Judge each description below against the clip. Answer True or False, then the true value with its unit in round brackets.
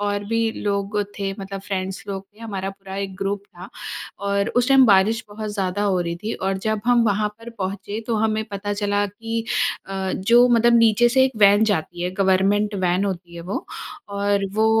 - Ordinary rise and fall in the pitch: False (2.2 semitones)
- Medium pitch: False (205 Hz)